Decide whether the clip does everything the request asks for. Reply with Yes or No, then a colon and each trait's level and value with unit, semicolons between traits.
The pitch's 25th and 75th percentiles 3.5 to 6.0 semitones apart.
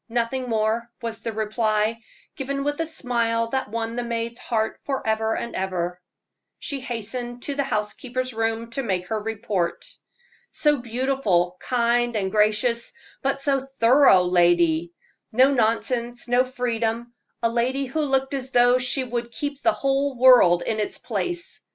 No: average, 3.0 semitones